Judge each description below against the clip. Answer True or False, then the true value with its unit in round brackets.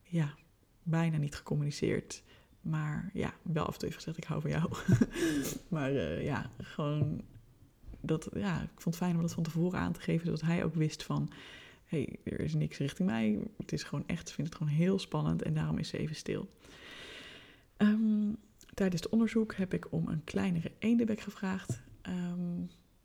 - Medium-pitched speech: True (165 Hz)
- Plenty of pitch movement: False (4.6 semitones)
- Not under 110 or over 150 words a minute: False (190 wpm)